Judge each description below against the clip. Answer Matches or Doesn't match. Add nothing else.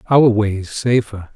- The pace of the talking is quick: Doesn't match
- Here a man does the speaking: Matches